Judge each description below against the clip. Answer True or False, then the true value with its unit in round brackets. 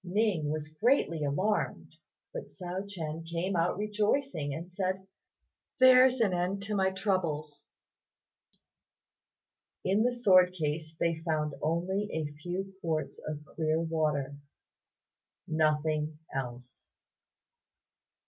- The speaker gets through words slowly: True (110 wpm)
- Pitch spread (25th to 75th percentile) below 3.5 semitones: False (4.2 semitones)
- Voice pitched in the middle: True (170 Hz)